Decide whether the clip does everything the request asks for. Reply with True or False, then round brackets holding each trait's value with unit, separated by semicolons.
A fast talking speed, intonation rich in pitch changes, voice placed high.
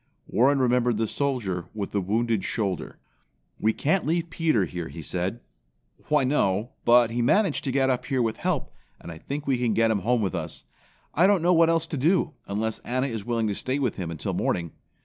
False (210 wpm; 5.7 semitones; 120 Hz)